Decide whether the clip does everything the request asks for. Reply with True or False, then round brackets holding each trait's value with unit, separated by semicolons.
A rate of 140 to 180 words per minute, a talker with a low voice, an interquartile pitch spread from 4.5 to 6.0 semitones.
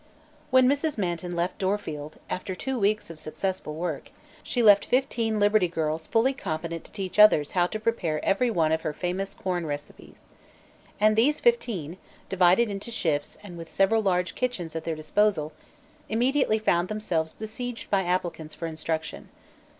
False (160 wpm; 185 Hz; 4.9 semitones)